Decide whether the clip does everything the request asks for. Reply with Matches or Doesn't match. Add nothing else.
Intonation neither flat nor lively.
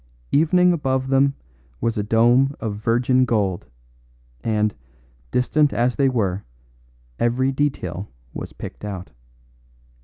Matches